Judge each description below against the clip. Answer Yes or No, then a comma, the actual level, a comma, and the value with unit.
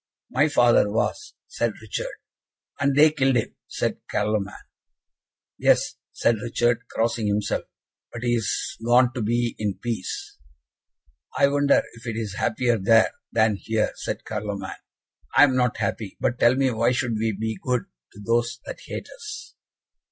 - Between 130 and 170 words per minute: Yes, average, 155 wpm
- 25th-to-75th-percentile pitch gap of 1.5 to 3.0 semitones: Yes, narrow, 2.6 semitones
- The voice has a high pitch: No, low, 120 Hz